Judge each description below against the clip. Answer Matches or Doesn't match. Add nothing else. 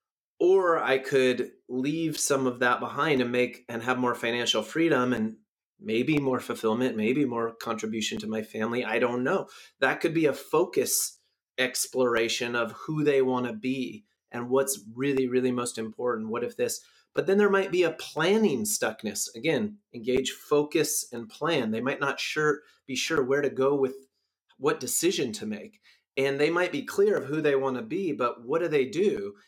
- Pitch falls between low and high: Doesn't match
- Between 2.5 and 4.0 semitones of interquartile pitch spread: Doesn't match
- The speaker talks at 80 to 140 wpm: Doesn't match